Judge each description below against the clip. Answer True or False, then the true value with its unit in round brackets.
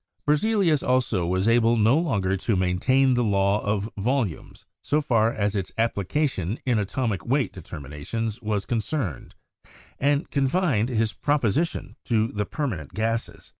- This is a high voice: False (115 Hz)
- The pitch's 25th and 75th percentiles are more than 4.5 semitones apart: True (5.1 semitones)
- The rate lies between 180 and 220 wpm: False (140 wpm)